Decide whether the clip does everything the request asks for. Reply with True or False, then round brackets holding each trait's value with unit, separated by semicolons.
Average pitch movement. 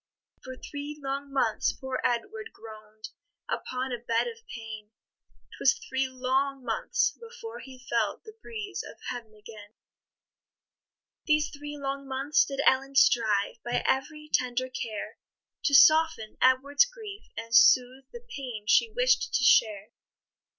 True (4.4 semitones)